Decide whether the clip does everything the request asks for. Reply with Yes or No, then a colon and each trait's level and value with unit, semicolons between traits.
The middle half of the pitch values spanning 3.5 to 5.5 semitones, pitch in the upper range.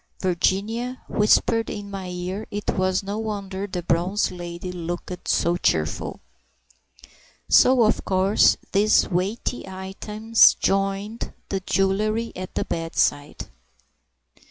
No: average, 2.8 semitones; high, 195 Hz